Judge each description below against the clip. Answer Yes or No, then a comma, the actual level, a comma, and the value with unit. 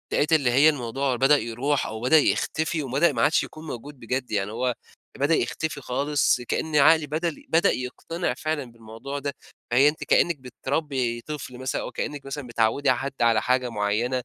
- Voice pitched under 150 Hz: Yes, low, 135 Hz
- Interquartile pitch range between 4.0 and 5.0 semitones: No, average, 3.4 semitones